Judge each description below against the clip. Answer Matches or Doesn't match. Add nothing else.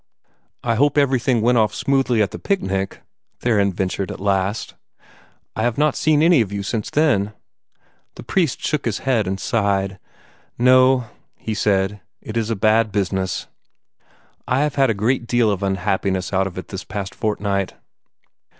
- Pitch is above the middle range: Doesn't match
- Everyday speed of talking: Matches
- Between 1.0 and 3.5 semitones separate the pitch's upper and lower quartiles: Doesn't match